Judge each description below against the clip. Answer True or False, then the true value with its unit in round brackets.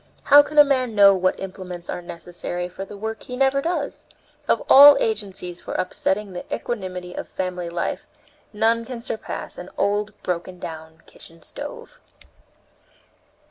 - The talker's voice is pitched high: True (195 Hz)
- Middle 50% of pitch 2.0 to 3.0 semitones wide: False (4.8 semitones)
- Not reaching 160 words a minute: True (150 wpm)